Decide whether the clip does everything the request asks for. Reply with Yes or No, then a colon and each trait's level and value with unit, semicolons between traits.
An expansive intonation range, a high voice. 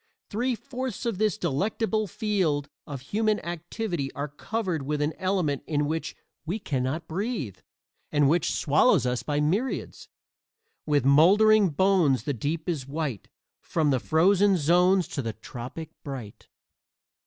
No: wide, 5.8 semitones; medium, 160 Hz